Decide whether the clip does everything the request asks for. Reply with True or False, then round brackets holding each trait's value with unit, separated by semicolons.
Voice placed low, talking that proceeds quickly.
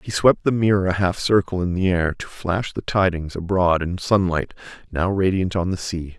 True (90 Hz; 215 wpm)